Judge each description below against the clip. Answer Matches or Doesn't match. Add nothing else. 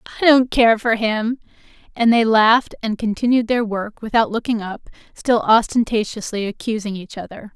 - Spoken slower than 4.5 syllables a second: Doesn't match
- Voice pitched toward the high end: Matches